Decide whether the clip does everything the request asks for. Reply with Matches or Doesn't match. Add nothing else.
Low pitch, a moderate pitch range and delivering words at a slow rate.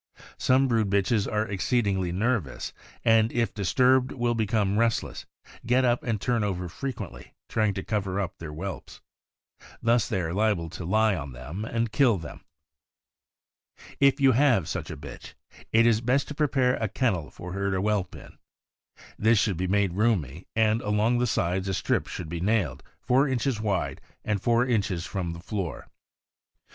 Doesn't match